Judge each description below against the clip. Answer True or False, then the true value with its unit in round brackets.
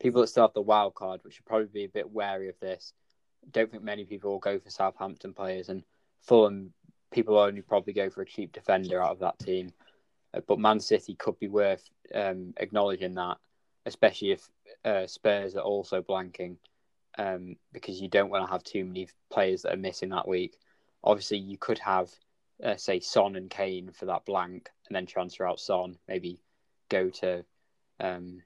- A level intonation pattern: True (1.8 semitones)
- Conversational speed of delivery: True (195 wpm)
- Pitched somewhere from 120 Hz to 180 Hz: False (95 Hz)